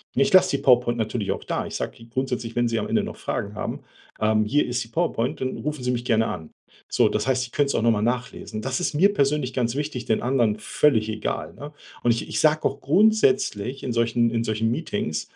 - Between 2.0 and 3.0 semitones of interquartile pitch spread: No, average, 3.5 semitones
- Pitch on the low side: Yes, low, 125 Hz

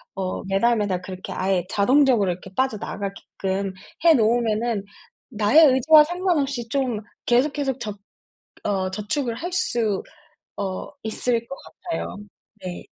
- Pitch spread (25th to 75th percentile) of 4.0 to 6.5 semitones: Yes, average, 5.3 semitones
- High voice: Yes, high, 225 Hz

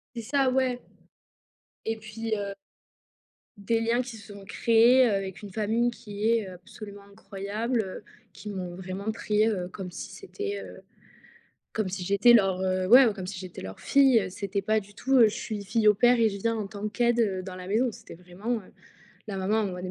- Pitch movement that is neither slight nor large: Yes, average, 3.1 semitones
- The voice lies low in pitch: No, high, 210 Hz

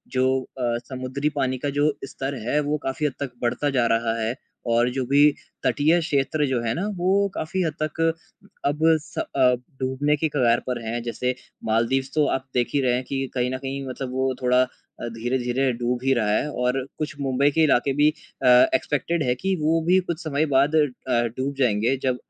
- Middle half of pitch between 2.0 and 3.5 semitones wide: Yes, average, 2.9 semitones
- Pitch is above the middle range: No, low, 135 Hz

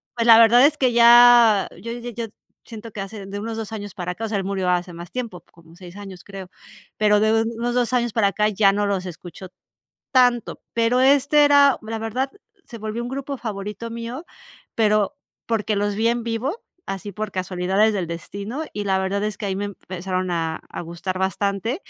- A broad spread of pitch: No, average, 3.4 semitones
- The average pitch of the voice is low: No, high, 210 Hz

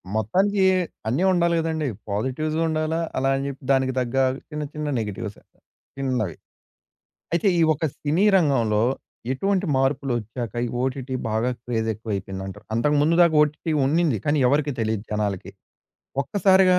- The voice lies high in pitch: No, low, 135 Hz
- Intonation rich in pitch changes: Yes, wide, 6.0 semitones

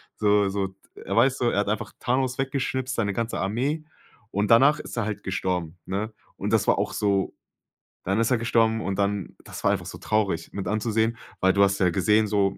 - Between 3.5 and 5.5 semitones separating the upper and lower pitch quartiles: No, average, 3.0 semitones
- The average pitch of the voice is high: No, low, 105 Hz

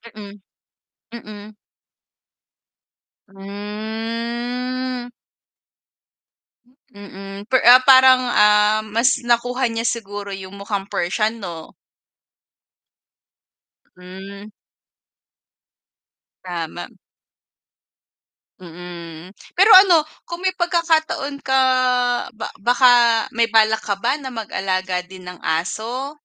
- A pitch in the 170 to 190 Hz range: No, high, 215 Hz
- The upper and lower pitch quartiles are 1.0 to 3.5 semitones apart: No, average, 4.2 semitones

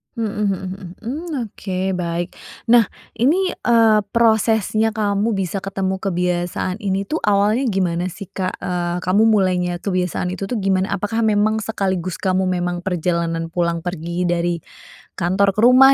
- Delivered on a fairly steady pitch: No, average, 3.4 semitones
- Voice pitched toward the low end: No, high, 190 Hz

